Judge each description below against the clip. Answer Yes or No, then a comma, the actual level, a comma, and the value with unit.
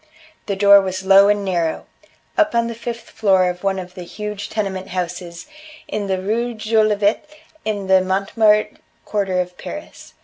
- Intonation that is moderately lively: No, narrow, 2.3 semitones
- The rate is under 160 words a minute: No, average, 165 wpm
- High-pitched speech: Yes, high, 200 Hz